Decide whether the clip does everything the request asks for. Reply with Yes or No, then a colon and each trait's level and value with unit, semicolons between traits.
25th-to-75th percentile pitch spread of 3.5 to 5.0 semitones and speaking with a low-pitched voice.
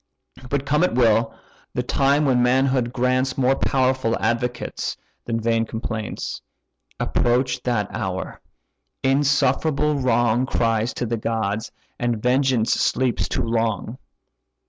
No: narrow, 2.5 semitones; low, 125 Hz